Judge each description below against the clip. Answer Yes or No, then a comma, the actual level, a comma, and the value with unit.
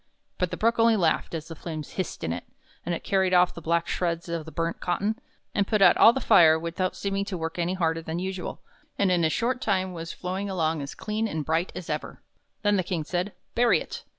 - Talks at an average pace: No, fast, 240 wpm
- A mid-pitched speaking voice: Yes, medium, 180 Hz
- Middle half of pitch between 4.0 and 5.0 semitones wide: No, average, 3.2 semitones